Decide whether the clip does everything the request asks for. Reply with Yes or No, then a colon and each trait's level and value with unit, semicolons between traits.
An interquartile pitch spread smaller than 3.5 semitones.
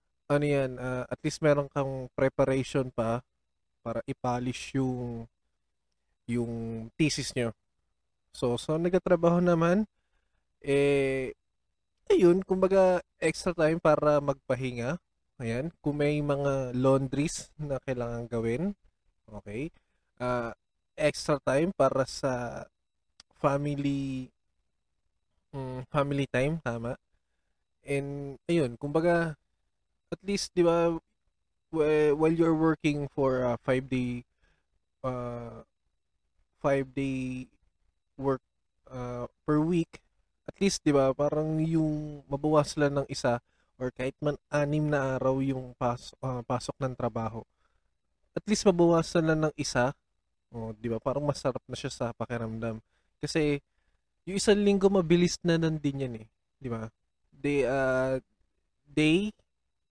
No: average, 4.3 semitones